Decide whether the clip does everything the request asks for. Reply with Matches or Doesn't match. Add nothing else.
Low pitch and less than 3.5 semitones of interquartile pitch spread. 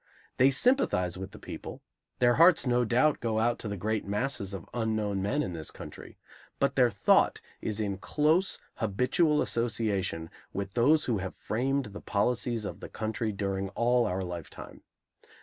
Doesn't match